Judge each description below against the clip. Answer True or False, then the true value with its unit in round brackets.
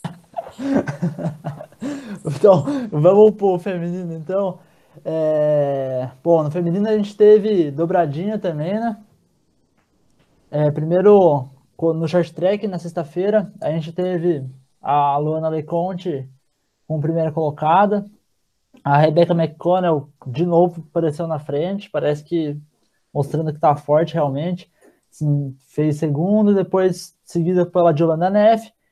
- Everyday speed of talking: False (110 wpm)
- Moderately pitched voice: True (170 Hz)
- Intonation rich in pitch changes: False (3.9 semitones)